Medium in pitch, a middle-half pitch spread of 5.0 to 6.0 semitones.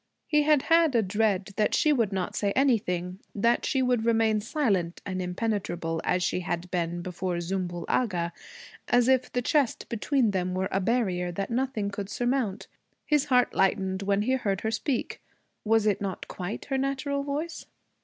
No: high, 210 Hz; average, 5.3 semitones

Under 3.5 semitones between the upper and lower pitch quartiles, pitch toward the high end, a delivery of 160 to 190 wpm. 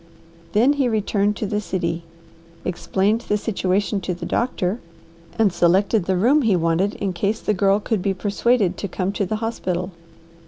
Yes: average, 2.9 semitones; high, 200 Hz; average, 170 wpm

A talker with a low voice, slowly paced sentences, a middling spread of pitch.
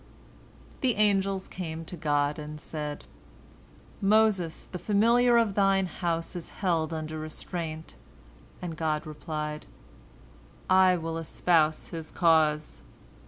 No: medium, 165 Hz; slow, 115 wpm; average, 3.6 semitones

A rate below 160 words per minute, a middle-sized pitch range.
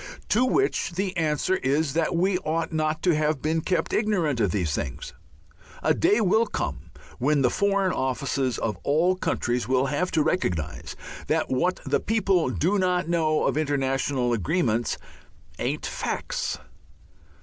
No: average, 150 wpm; wide, 5.7 semitones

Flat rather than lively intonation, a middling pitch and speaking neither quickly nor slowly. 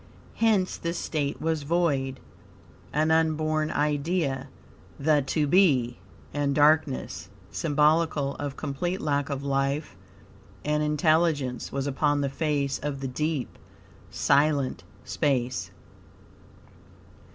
No: narrow, 2.3 semitones; medium, 145 Hz; slow, 105 wpm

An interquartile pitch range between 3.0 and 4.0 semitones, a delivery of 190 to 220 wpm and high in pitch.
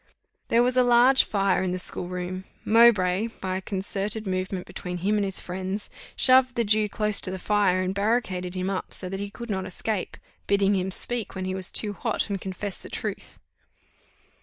No: narrow, 2.6 semitones; average, 200 wpm; high, 195 Hz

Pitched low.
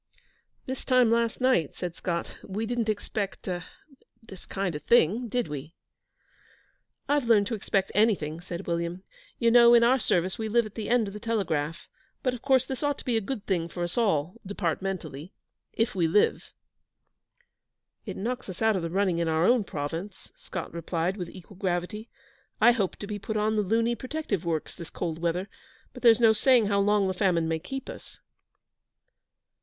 No: high, 200 Hz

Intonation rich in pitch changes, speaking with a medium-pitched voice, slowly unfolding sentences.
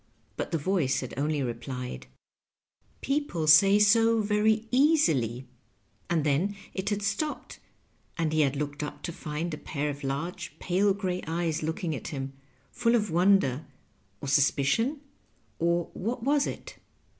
No: wide, 6.4 semitones; medium, 170 Hz; average, 155 wpm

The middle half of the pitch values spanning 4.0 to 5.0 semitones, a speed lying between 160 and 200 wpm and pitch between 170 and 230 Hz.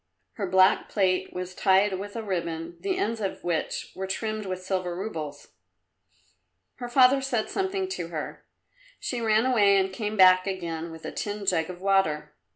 No: average, 3.2 semitones; average, 170 wpm; high, 190 Hz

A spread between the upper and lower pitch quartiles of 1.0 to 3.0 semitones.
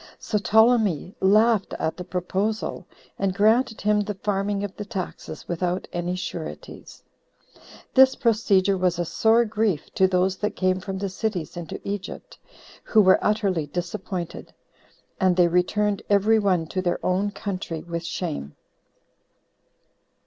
Yes: average, 2.7 semitones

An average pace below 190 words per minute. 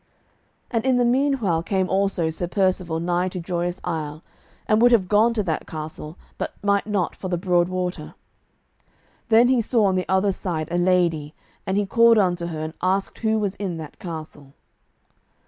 Yes: average, 180 wpm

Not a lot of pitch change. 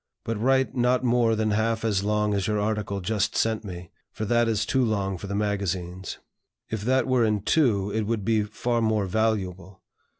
Yes: narrow, 2.3 semitones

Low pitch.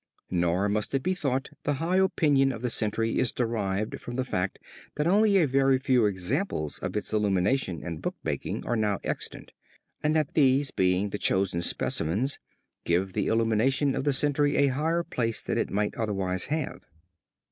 Yes: low, 120 Hz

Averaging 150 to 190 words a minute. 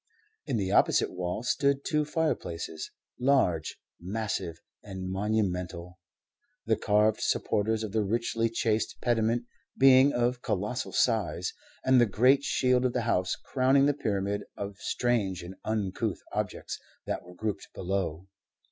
No: slow, 135 wpm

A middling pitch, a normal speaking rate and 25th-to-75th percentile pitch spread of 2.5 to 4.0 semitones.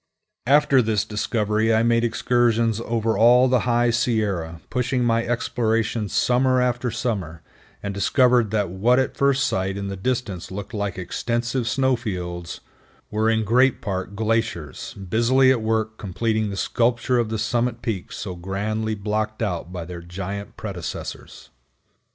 No: low, 110 Hz; average, 150 wpm; average, 3.4 semitones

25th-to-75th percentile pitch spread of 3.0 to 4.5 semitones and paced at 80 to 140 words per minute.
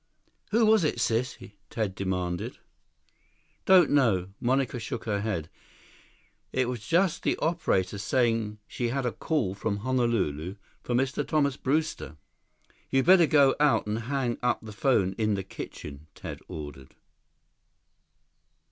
No: wide, 5.5 semitones; slow, 135 wpm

